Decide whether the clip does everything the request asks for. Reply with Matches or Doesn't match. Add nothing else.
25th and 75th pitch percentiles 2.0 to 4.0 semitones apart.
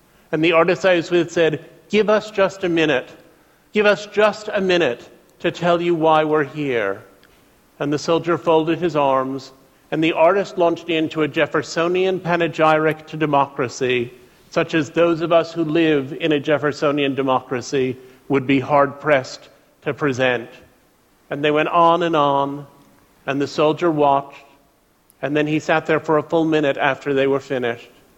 Matches